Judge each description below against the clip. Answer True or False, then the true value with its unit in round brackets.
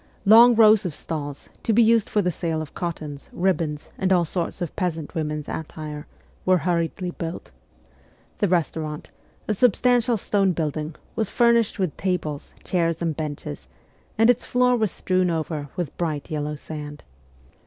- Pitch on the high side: False (170 Hz)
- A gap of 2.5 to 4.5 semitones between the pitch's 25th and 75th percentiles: False (4.9 semitones)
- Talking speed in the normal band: True (155 wpm)